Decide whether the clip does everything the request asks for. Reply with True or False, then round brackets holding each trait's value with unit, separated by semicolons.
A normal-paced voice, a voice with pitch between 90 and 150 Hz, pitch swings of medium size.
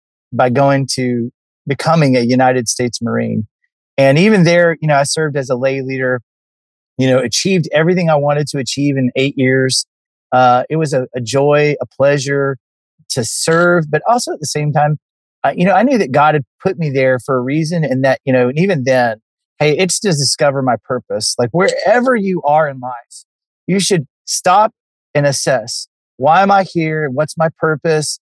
True (195 wpm; 140 Hz; 4.0 semitones)